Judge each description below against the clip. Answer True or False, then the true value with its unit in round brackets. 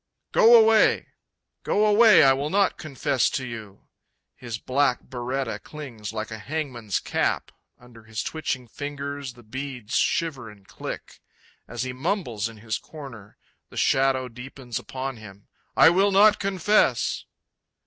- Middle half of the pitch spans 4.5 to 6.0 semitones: True (5.2 semitones)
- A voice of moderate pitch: False (130 Hz)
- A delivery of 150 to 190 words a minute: False (140 wpm)